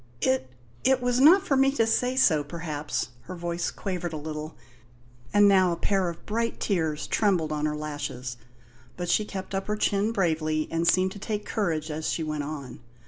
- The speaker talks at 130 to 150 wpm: No, average, 195 wpm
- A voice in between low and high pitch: Yes, medium, 175 Hz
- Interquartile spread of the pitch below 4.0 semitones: No, average, 5.1 semitones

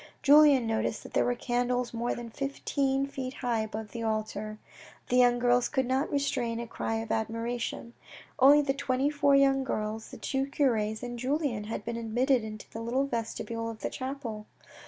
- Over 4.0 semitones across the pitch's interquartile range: No, average, 3.2 semitones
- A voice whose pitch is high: Yes, high, 245 Hz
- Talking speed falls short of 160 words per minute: No, average, 180 wpm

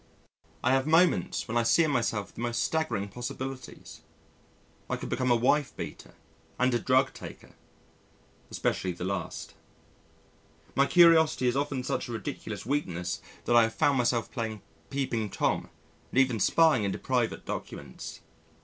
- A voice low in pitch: Yes, low, 125 Hz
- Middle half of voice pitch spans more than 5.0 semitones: No, average, 3.7 semitones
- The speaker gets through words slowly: No, average, 150 wpm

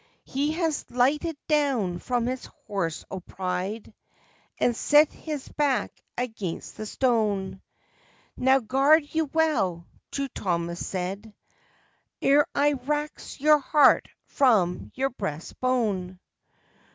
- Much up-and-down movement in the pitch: Yes, wide, 7.1 semitones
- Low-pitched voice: No, very high, 250 Hz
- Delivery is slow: Yes, slow, 115 wpm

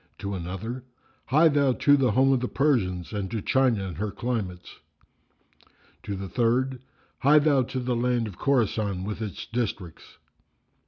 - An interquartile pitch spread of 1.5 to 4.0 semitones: No, average, 4.8 semitones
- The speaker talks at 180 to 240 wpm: No, average, 160 wpm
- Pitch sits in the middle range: No, low, 120 Hz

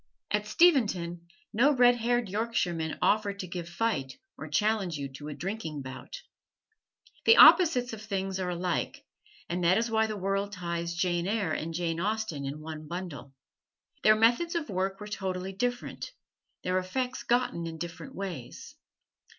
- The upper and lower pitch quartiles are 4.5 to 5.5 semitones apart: Yes, average, 4.8 semitones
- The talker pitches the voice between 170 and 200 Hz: Yes, high, 190 Hz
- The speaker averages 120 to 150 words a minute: No, average, 160 wpm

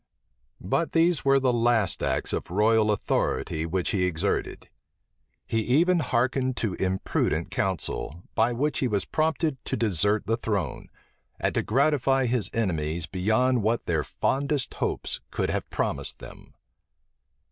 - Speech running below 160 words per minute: Yes, average, 140 wpm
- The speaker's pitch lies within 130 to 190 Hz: No, low, 115 Hz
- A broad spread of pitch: Yes, wide, 5.8 semitones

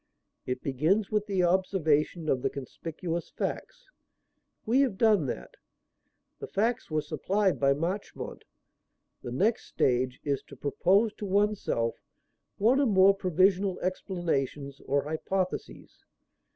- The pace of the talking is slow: Yes, slow, 125 wpm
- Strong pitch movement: Yes, wide, 6.0 semitones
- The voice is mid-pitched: Yes, medium, 180 Hz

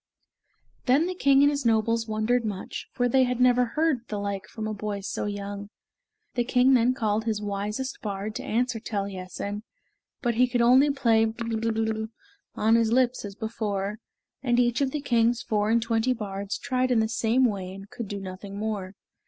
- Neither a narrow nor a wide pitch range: Yes, average, 3.1 semitones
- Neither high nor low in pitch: No, high, 225 Hz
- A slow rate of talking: No, average, 185 wpm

